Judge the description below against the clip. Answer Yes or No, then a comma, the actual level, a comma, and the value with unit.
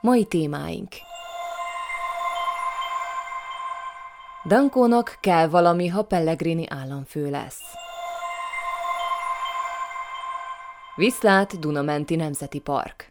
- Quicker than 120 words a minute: No, slow, 60 wpm